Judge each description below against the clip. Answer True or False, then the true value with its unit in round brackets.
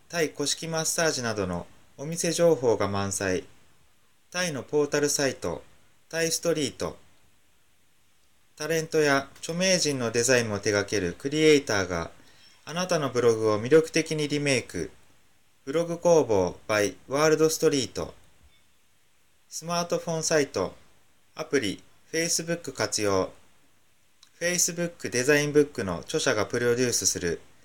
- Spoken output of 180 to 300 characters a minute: True (270 characters per minute)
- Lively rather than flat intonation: True (7.2 semitones)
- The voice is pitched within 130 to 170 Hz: True (140 Hz)